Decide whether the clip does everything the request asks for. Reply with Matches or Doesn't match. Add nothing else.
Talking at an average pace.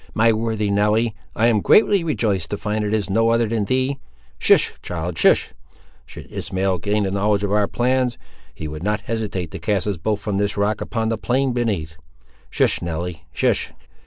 Matches